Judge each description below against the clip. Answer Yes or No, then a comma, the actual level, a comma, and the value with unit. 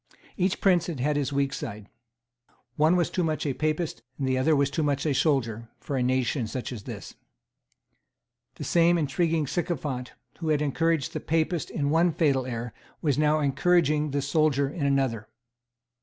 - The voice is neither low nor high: Yes, medium, 145 Hz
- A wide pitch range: No, average, 3.4 semitones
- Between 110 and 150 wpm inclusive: No, average, 170 wpm